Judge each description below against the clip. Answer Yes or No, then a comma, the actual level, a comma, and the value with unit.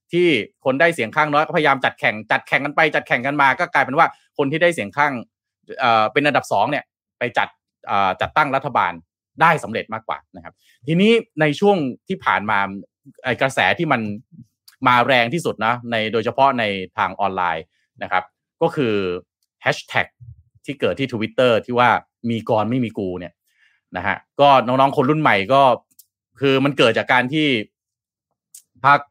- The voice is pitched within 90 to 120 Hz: No, low, 130 Hz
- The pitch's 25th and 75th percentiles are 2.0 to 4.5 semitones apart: No, wide, 5.5 semitones